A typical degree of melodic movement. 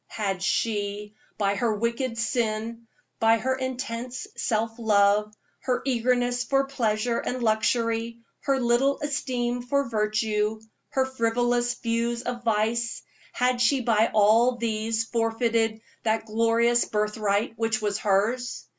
No: narrow, 2.1 semitones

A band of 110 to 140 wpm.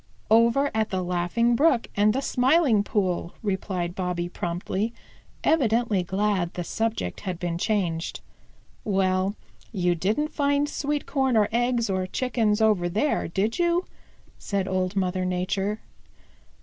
Yes: slow, 135 wpm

